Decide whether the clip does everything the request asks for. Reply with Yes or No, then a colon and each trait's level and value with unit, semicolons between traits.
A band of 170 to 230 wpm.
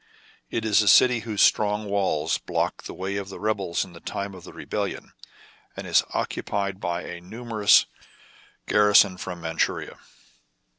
No: average, 160 wpm